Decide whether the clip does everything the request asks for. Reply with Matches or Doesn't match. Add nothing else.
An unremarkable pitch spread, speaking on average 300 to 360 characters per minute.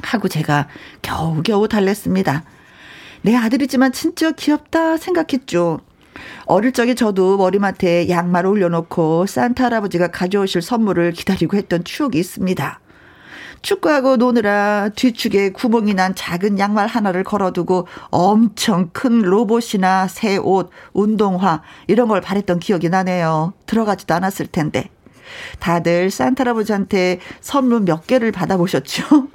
Matches